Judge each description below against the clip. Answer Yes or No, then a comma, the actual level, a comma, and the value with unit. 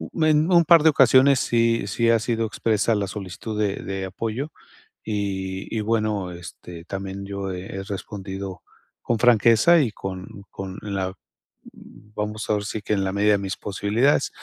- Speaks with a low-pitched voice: Yes, low, 105 Hz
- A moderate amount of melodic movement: Yes, average, 3.0 semitones